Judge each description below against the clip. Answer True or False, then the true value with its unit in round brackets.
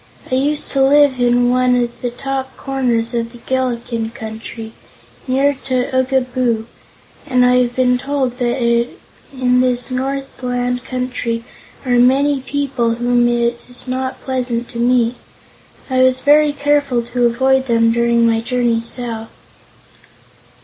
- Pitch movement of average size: False (1.7 semitones)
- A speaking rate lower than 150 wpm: True (140 wpm)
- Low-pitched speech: False (250 Hz)